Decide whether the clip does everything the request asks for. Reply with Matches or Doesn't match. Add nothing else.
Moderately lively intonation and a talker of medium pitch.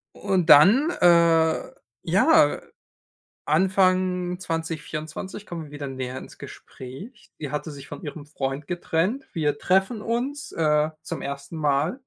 Matches